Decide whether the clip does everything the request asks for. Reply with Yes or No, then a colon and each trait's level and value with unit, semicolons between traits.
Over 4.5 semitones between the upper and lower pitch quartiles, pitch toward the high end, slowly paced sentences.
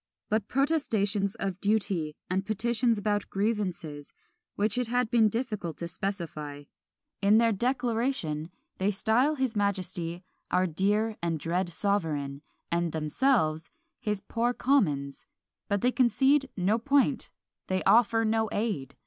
Yes: average, 5.1 semitones; high, 205 Hz; slow, 130 wpm